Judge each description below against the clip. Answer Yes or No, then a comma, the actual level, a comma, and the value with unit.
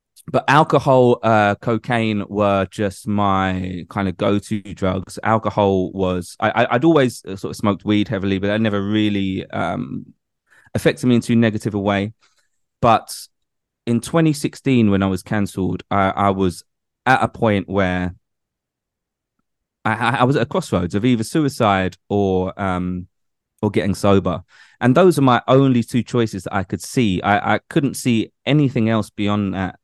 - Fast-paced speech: No, average, 165 wpm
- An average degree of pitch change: Yes, average, 3.6 semitones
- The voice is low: Yes, low, 105 Hz